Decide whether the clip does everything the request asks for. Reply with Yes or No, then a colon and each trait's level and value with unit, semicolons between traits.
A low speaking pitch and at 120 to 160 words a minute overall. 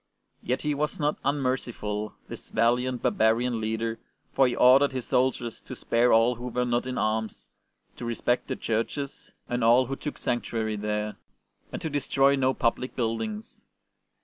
No: low, 120 Hz; average, 175 wpm